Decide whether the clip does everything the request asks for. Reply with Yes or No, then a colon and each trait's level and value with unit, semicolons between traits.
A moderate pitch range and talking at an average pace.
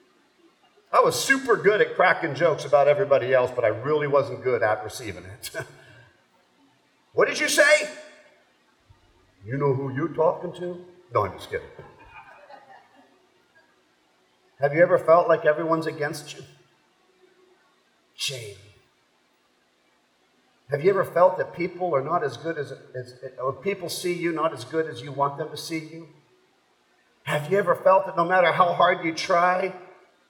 Yes: average, 4.8 semitones; average, 155 wpm